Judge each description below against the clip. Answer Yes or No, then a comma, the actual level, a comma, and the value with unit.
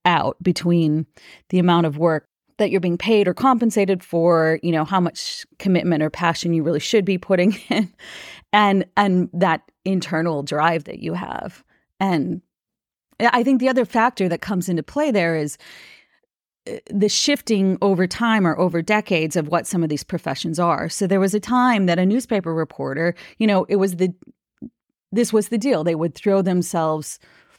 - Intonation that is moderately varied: Yes, average, 3.8 semitones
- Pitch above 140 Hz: Yes, medium, 185 Hz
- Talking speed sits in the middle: Yes, average, 180 wpm